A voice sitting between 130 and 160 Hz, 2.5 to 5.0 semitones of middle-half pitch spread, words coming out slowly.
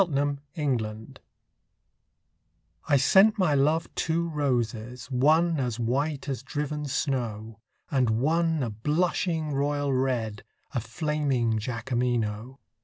Yes: low, 135 Hz; average, 4.2 semitones; slow, 110 wpm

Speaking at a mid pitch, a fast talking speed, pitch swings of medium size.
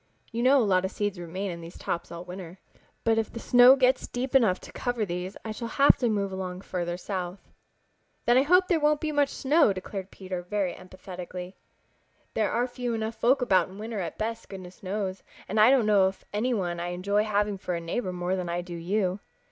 No: high, 200 Hz; fast, 220 wpm; average, 4.4 semitones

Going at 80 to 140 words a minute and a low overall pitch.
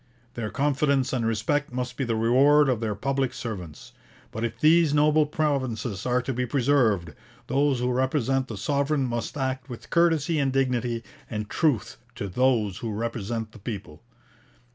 No: average, 165 wpm; low, 125 Hz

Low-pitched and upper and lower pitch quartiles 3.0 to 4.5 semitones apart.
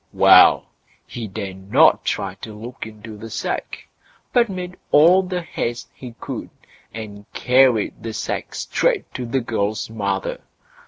Yes: low, 115 Hz; average, 4.0 semitones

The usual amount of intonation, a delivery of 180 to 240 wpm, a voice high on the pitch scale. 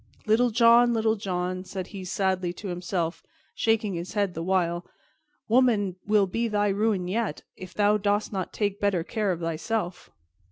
No: average, 3.2 semitones; average, 165 wpm; high, 200 Hz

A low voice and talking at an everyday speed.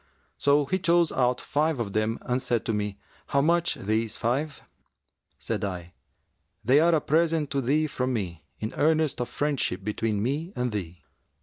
Yes: low, 125 Hz; average, 175 wpm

